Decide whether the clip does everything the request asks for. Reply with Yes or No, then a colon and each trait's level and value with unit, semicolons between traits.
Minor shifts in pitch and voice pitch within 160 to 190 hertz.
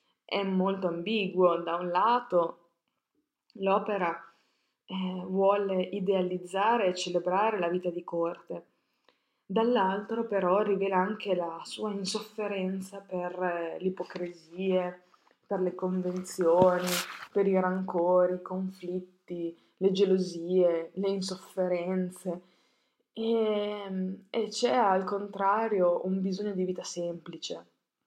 Yes: narrow, 1.8 semitones; medium, 185 Hz